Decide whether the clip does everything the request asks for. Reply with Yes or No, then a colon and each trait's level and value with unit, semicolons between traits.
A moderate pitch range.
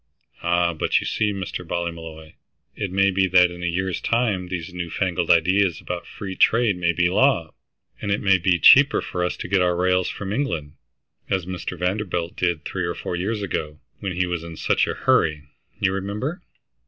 No: narrow, 2.3 semitones